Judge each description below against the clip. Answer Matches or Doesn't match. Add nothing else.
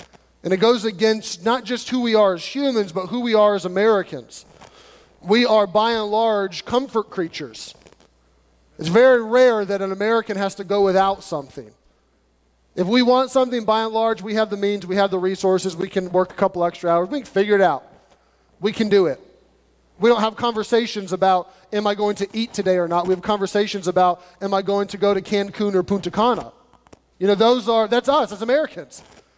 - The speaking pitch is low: Doesn't match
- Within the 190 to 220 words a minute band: Matches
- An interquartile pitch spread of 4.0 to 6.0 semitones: Doesn't match